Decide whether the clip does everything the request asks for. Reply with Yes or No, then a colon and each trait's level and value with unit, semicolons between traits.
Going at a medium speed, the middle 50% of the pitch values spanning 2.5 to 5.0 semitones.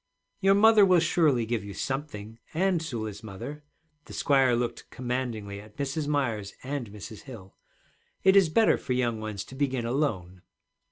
No: average, 160 wpm; wide, 5.6 semitones